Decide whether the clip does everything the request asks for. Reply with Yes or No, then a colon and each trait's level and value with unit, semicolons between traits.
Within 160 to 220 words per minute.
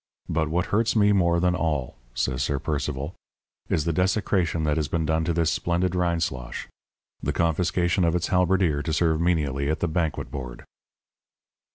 Yes: average, 170 wpm